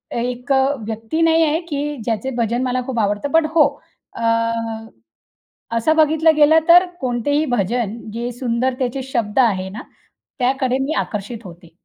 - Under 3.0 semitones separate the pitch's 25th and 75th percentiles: No, average, 4.2 semitones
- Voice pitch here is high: Yes, very high, 250 Hz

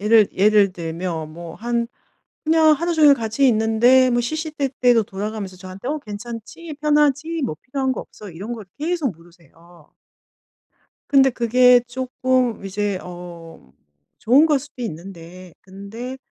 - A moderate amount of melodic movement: No, wide, 6.0 semitones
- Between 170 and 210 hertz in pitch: No, high, 230 Hz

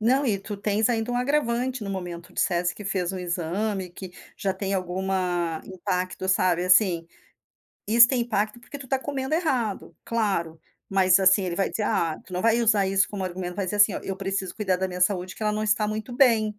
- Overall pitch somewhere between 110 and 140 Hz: No, high, 195 Hz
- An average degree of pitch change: Yes, average, 3.4 semitones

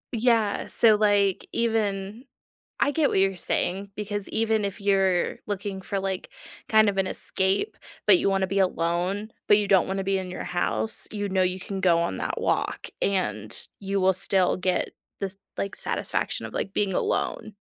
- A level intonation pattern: Yes, narrow, 1.7 semitones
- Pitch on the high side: Yes, high, 195 Hz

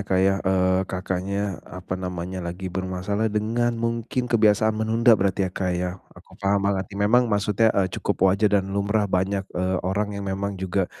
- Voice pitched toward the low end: Yes, low, 100 Hz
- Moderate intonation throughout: No, narrow, 2.2 semitones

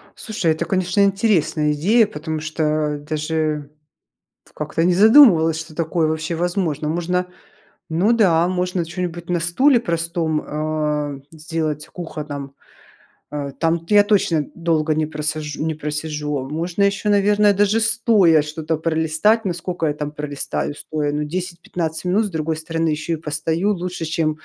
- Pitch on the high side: No, medium, 160 Hz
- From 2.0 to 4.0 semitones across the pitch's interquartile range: Yes, average, 2.9 semitones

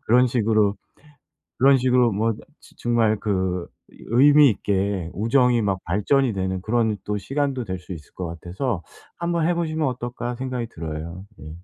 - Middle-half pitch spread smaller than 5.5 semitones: Yes, average, 5.1 semitones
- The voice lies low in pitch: Yes, low, 110 Hz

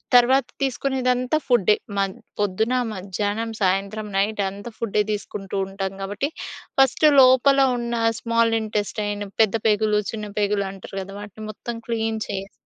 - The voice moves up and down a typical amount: Yes, average, 3.0 semitones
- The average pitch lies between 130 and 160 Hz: No, high, 210 Hz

